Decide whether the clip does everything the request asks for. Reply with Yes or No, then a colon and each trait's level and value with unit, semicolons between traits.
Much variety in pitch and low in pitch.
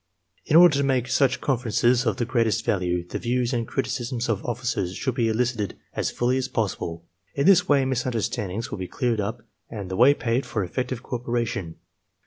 No: average, 2.8 semitones; low, 120 Hz